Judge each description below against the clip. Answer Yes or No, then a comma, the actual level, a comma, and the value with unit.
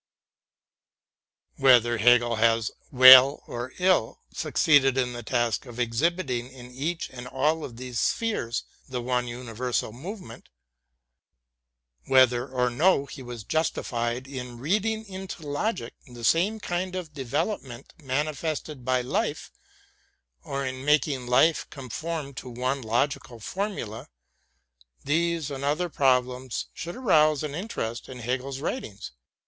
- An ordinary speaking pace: No, slow, 130 wpm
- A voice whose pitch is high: No, low, 130 Hz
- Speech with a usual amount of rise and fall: Yes, average, 4.1 semitones